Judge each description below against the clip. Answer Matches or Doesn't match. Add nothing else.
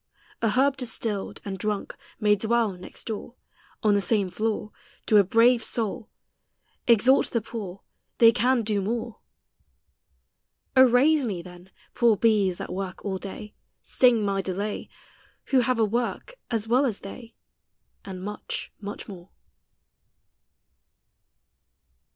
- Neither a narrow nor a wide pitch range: Matches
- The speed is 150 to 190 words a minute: Doesn't match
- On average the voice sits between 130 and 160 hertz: Doesn't match